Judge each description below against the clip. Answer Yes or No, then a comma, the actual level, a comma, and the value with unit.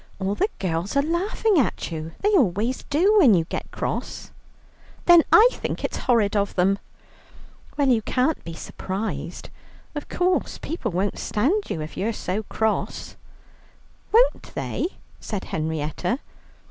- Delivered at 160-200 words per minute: No, average, 145 wpm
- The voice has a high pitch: Yes, high, 225 Hz